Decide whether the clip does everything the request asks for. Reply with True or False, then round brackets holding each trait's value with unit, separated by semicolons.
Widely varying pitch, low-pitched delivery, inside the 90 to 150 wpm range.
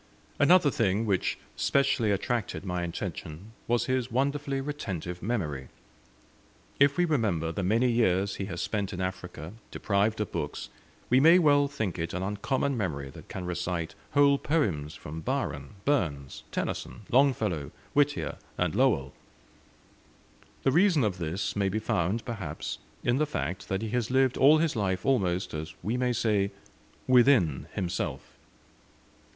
True (7.0 semitones; 105 Hz; 145 wpm)